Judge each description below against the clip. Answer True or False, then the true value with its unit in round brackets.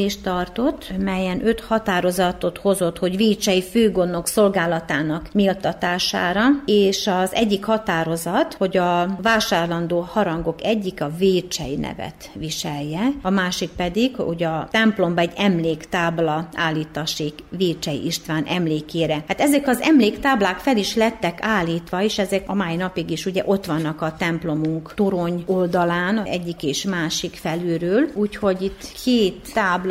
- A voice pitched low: False (180 Hz)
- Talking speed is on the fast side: False (130 wpm)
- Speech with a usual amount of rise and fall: True (3.5 semitones)